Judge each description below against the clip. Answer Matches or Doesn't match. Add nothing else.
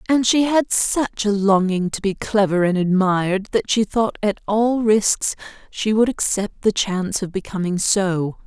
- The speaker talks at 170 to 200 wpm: Matches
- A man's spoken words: Doesn't match